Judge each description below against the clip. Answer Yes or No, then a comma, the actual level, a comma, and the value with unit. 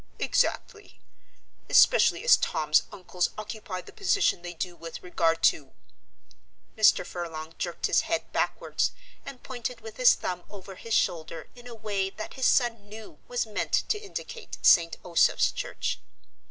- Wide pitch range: Yes, wide, 5.9 semitones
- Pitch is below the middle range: No, high, 205 Hz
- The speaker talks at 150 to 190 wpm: Yes, average, 155 wpm